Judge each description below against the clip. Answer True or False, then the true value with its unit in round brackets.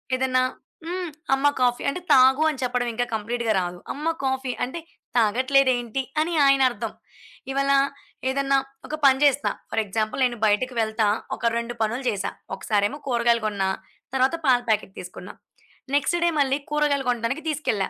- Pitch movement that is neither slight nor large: True (3.1 semitones)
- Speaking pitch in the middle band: False (255 Hz)